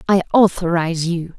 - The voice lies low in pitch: No, medium, 175 Hz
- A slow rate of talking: Yes, slow, 130 wpm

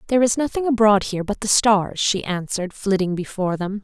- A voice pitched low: No, high, 205 Hz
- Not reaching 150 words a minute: No, fast, 205 wpm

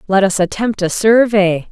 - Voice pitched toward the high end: Yes, high, 200 Hz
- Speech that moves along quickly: No, average, 175 wpm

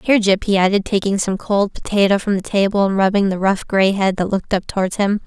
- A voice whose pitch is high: Yes, high, 195 Hz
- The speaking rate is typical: No, fast, 250 wpm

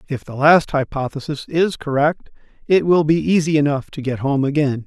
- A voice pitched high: No, medium, 145 Hz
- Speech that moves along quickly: No, average, 185 wpm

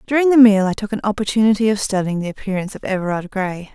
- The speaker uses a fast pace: Yes, fast, 225 wpm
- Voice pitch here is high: Yes, high, 205 Hz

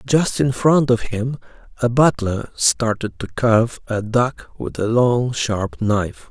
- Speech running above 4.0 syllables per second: No, 3.8 syllables/s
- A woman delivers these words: No, male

